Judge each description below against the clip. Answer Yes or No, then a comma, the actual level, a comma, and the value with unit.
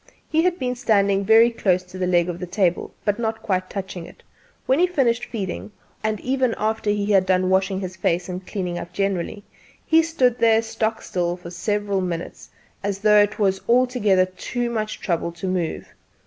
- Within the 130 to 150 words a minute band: No, average, 190 wpm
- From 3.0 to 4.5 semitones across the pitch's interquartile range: Yes, average, 3.5 semitones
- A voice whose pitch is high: Yes, high, 200 Hz